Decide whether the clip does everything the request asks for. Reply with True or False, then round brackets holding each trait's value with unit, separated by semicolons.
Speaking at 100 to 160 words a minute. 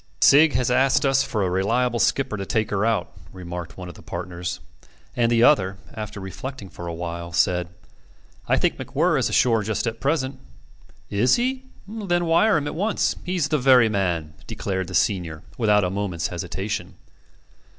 False (175 wpm)